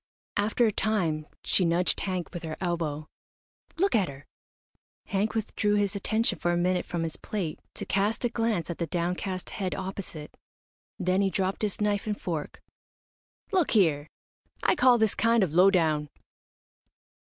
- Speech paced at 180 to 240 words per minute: No, average, 165 wpm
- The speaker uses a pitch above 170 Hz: Yes, high, 190 Hz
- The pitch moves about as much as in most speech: Yes, average, 3.8 semitones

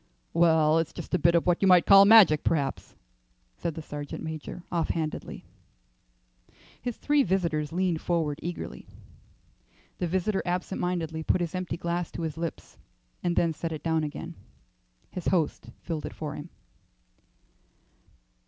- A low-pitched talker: No, medium, 170 Hz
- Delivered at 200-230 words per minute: No, average, 150 wpm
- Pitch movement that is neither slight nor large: No, narrow, 2.2 semitones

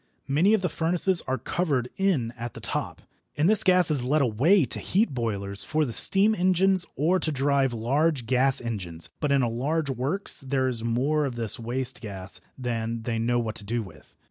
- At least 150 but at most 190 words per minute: No, average, 200 wpm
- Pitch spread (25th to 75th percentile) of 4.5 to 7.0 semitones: Yes, wide, 5.6 semitones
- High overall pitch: No, low, 130 Hz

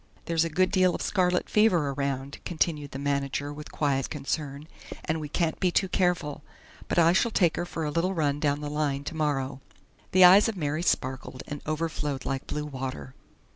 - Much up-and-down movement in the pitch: No, average, 3.7 semitones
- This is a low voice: No, medium, 150 Hz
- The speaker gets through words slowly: No, average, 190 wpm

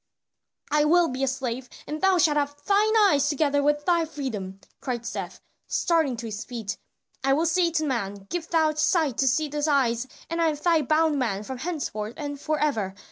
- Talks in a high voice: Yes, very high, 290 Hz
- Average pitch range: Yes, average, 4.1 semitones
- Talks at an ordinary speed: Yes, average, 190 wpm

